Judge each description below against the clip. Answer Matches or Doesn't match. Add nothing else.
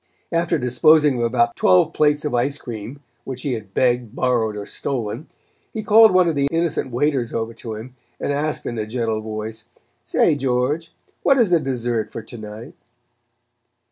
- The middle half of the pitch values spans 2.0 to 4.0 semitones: Doesn't match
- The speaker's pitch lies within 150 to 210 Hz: Doesn't match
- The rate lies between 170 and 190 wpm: Matches